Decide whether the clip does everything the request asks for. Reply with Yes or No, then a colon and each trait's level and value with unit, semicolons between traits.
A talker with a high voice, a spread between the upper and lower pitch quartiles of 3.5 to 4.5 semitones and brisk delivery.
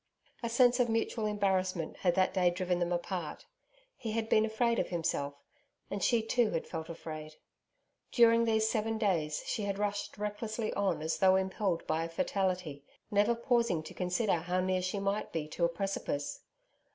No: high, 195 Hz; average, 4.1 semitones; average, 175 wpm